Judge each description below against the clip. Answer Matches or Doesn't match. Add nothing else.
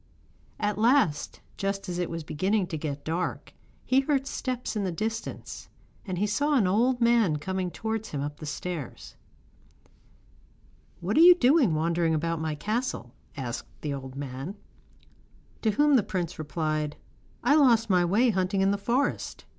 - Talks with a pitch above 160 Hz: Matches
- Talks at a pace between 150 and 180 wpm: Matches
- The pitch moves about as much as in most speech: Doesn't match